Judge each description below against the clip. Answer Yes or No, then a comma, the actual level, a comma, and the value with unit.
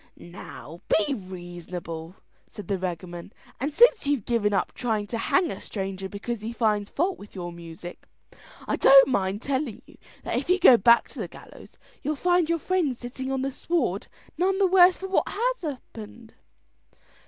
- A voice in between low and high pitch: No, high, 235 Hz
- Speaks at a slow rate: No, average, 175 wpm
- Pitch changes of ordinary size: No, wide, 8.1 semitones